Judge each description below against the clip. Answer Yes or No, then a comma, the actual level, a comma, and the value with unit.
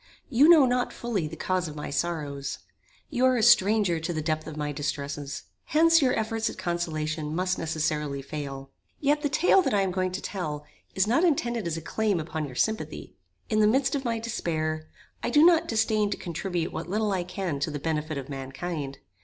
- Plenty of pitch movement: Yes, wide, 6.5 semitones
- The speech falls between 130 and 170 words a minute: No, fast, 205 wpm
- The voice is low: No, medium, 175 Hz